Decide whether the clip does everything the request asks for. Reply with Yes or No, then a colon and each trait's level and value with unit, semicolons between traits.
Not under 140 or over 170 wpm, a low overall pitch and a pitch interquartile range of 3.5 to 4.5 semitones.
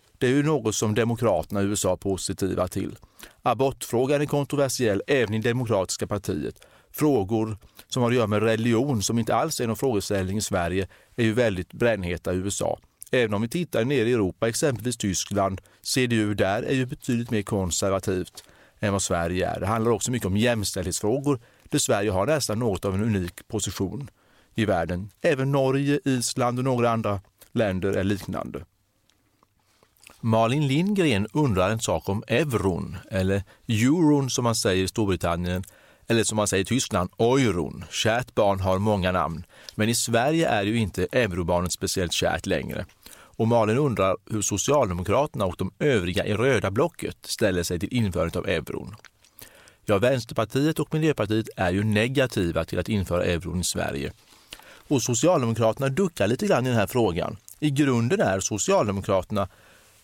Yes: average, 165 wpm; low, 110 Hz; average, 4.2 semitones